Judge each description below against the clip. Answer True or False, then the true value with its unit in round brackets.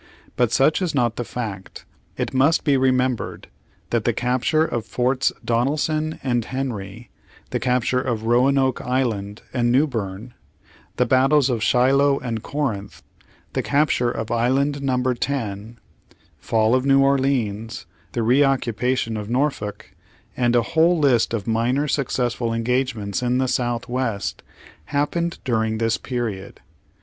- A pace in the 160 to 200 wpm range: False (140 wpm)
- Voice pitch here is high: False (125 Hz)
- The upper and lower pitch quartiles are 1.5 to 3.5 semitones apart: True (3.0 semitones)